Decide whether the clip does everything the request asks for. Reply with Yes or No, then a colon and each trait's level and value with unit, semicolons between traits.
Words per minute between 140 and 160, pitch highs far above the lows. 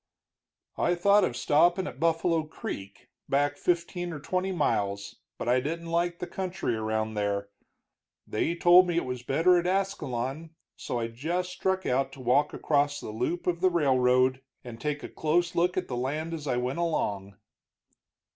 No: average, 175 wpm; wide, 5.7 semitones